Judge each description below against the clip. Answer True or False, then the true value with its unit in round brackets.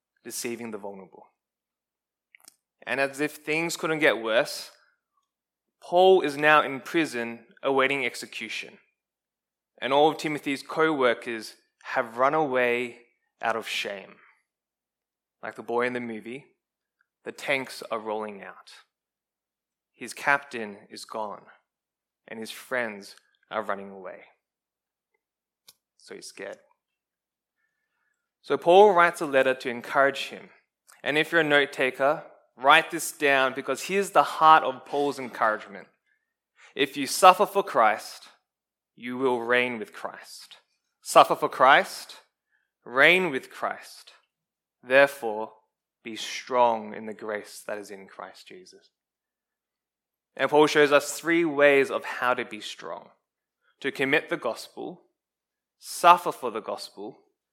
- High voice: False (135 Hz)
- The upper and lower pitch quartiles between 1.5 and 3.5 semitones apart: False (4.5 semitones)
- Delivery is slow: True (130 wpm)